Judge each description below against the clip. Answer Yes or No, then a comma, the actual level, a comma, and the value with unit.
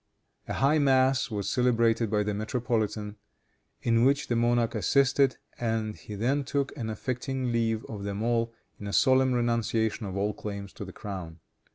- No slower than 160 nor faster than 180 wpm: Yes, average, 170 wpm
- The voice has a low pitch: Yes, low, 115 Hz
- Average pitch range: Yes, average, 3.6 semitones